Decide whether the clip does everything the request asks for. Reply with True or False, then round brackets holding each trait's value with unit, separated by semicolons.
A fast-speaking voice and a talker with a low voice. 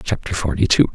False (190 wpm; 80 Hz)